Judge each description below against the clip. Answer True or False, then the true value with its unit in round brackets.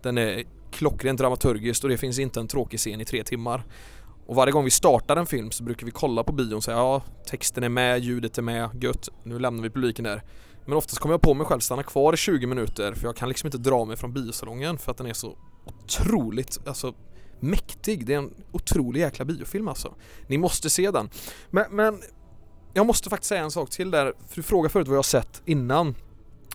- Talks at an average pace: False (230 wpm)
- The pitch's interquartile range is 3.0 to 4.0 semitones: True (3.7 semitones)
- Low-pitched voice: True (125 Hz)